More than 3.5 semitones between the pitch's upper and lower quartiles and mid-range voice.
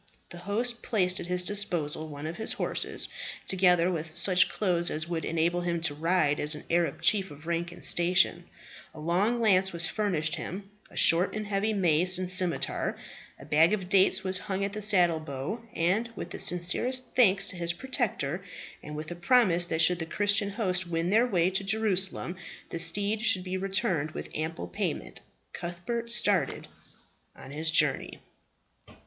No: average, 3.2 semitones; medium, 180 Hz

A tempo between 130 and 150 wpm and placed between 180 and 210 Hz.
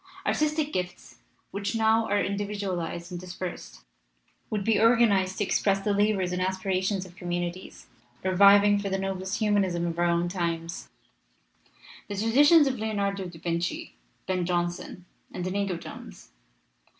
Yes: average, 140 wpm; high, 190 Hz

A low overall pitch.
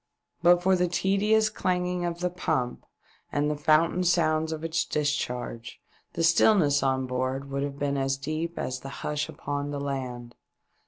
No: medium, 150 Hz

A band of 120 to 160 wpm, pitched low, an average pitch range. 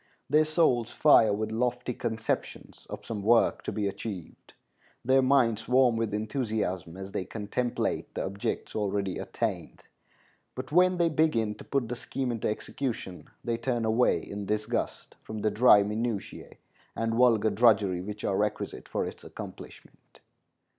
Yes: average, 150 wpm; low, 115 Hz; average, 3.2 semitones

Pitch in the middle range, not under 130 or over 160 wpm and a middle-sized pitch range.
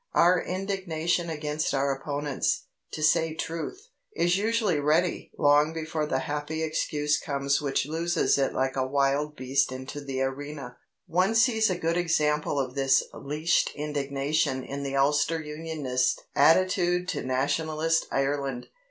Yes: medium, 150 Hz; average, 140 wpm; average, 3.0 semitones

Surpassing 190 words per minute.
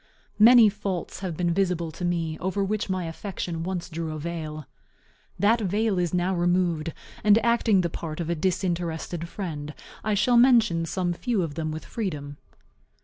No: average, 170 wpm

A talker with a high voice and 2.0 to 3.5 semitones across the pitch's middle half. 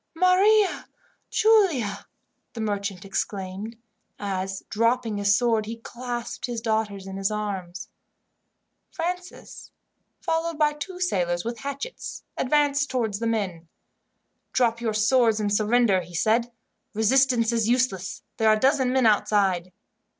No: high, 225 Hz; average, 4.6 semitones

